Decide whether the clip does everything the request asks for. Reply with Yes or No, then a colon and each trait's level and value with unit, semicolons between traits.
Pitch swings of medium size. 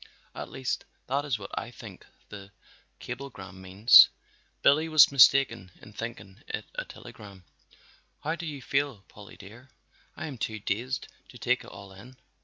No: wide, 5.7 semitones